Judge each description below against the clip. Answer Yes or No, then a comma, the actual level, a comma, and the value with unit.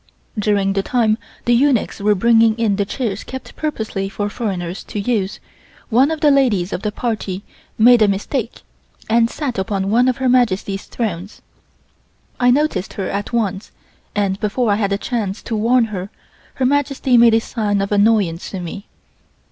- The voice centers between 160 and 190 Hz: No, high, 215 Hz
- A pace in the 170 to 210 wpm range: Yes, average, 175 wpm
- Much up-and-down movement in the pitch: No, average, 3.5 semitones